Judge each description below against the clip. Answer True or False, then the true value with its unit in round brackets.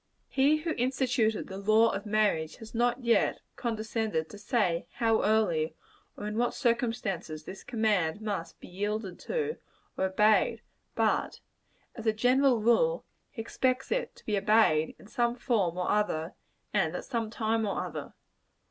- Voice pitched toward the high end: True (220 Hz)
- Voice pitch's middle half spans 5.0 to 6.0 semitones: False (3.3 semitones)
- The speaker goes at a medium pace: True (155 wpm)